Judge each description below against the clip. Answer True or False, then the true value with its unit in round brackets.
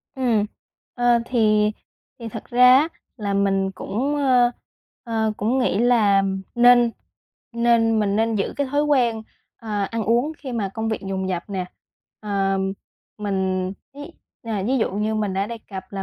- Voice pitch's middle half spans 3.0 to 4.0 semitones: True (3.4 semitones)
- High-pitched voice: True (220 Hz)